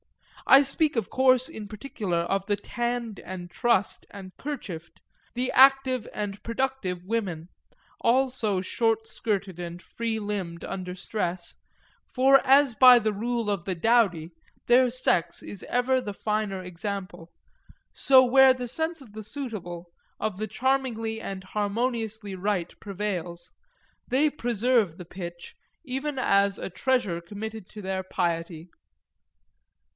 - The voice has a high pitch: Yes, high, 215 Hz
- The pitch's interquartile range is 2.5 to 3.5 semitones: No, average, 5.0 semitones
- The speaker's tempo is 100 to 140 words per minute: Yes, slow, 135 wpm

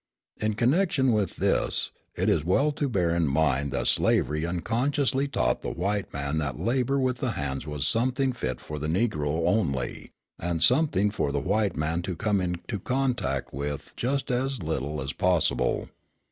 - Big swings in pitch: Yes, wide, 8.8 semitones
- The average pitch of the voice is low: Yes, very low, 90 Hz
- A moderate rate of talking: Yes, average, 170 wpm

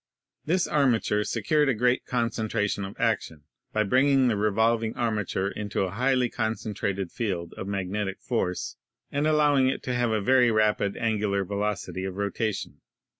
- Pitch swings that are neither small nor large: Yes, average, 3.7 semitones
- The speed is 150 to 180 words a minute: Yes, average, 155 wpm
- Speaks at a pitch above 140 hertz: No, low, 110 Hz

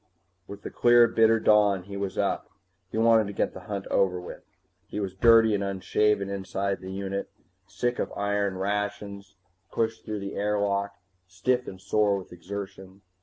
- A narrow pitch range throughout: Yes, narrow, 1.5 semitones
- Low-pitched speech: Yes, low, 100 Hz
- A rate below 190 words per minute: Yes, average, 170 wpm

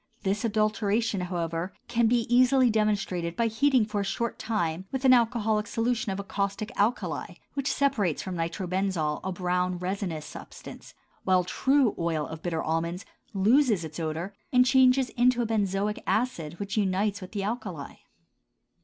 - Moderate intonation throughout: Yes, average, 4.5 semitones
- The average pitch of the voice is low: No, high, 200 Hz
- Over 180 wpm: No, average, 155 wpm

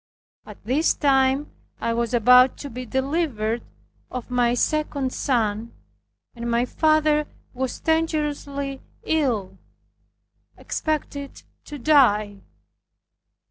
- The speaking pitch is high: Yes, very high, 260 Hz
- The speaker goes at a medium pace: No, slow, 100 wpm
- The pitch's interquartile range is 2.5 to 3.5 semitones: No, average, 4.0 semitones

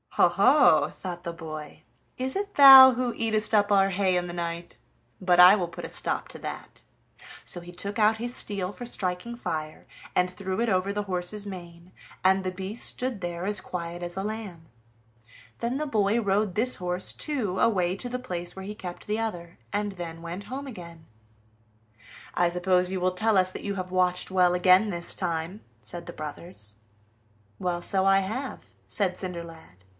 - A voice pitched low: No, medium, 185 Hz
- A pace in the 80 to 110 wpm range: No, average, 190 wpm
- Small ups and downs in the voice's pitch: No, average, 3.3 semitones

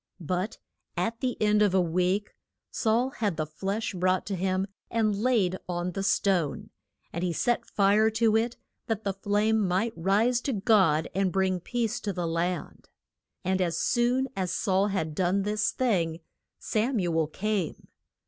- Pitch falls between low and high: No, high, 195 Hz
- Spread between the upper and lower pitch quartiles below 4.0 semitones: Yes, average, 3.5 semitones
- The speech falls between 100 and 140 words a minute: No, average, 165 wpm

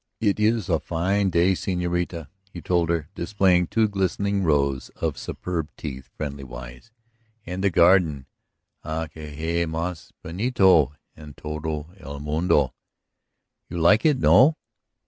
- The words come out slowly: Yes, slow, 130 wpm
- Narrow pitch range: No, average, 3.9 semitones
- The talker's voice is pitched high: No, very low, 85 Hz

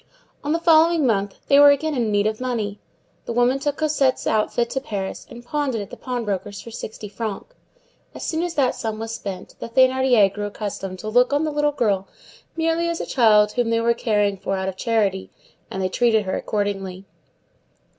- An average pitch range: Yes, average, 5.0 semitones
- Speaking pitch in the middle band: No, high, 230 Hz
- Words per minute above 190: Yes, fast, 205 wpm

